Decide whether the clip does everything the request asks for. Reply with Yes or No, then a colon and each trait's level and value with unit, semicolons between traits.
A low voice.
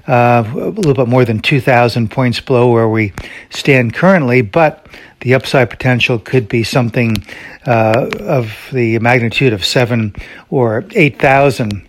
Yes: low, 120 Hz